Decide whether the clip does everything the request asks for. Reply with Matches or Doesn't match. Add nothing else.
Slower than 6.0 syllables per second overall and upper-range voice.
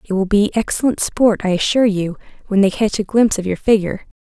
Doesn't match